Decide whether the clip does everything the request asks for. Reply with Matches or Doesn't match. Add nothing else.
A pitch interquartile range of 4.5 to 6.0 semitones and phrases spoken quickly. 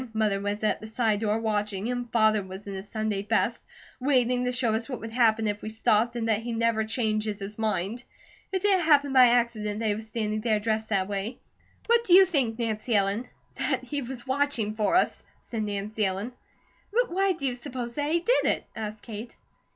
Doesn't match